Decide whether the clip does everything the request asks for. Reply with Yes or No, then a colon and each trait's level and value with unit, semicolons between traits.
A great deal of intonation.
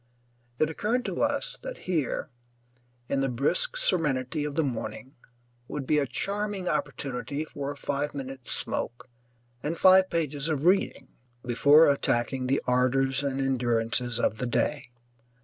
No: average, 3.9 semitones